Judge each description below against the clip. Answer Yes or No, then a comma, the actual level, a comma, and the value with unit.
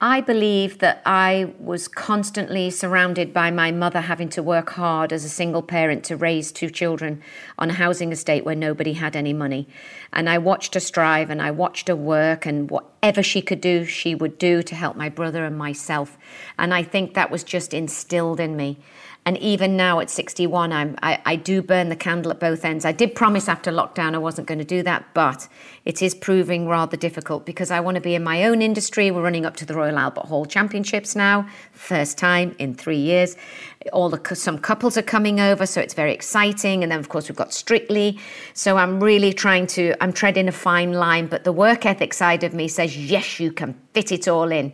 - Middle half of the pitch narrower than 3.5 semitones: Yes, average, 2.8 semitones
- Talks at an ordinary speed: No, fast, 220 wpm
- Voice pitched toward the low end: No, medium, 175 Hz